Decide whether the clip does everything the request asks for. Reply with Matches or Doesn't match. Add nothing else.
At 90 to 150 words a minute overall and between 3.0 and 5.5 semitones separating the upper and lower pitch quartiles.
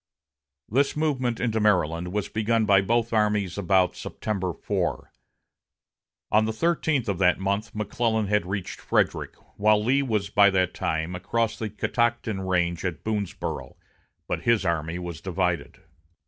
Matches